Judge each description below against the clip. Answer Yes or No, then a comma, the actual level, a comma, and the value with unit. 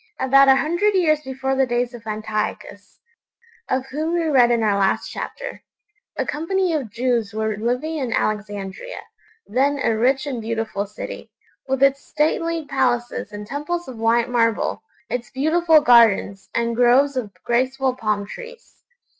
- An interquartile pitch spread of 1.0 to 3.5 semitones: No, average, 4.5 semitones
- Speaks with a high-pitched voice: Yes, very high, 255 Hz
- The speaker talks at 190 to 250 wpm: No, average, 155 wpm